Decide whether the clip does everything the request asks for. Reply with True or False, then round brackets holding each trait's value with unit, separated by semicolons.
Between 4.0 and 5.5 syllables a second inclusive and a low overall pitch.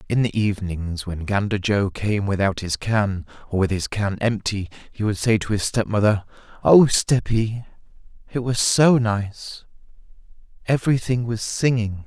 True (4.5 syllables/s; 105 Hz)